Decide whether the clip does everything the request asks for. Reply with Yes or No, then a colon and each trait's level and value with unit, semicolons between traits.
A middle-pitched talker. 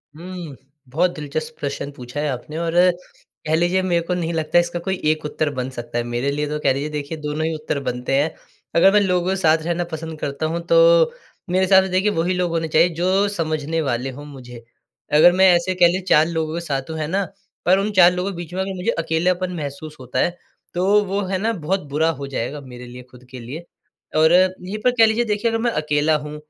Yes: medium, 160 Hz